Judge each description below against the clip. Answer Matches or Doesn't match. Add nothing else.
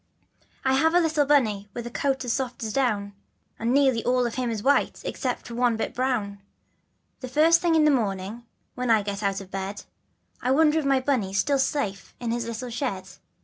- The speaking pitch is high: Matches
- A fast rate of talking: Matches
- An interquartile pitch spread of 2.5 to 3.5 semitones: Doesn't match